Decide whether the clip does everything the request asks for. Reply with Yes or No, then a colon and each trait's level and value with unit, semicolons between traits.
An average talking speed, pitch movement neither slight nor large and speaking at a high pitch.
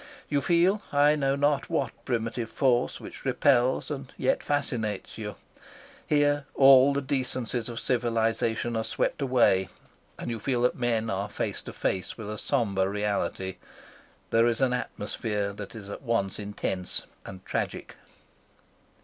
No: average, 150 wpm; average, 4.4 semitones; low, 120 Hz